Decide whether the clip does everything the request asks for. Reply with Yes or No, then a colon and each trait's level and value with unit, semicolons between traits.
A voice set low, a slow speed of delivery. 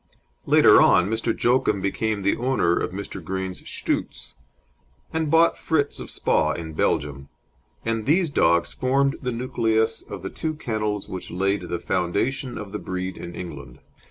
No: low, 105 Hz; average, 155 wpm